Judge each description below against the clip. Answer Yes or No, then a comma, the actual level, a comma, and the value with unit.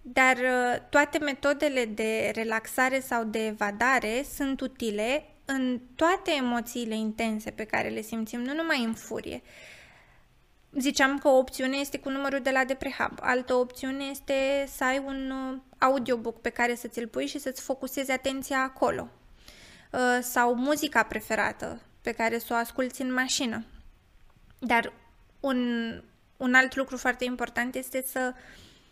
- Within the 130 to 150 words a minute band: Yes, average, 140 wpm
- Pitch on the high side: Yes, very high, 255 Hz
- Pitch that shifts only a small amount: Yes, narrow, 2.3 semitones